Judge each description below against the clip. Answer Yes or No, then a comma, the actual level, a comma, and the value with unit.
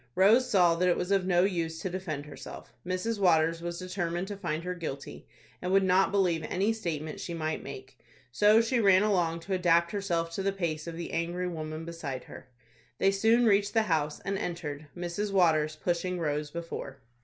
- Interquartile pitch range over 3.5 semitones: No, average, 3.0 semitones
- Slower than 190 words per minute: No, average, 195 wpm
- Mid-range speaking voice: Yes, medium, 175 Hz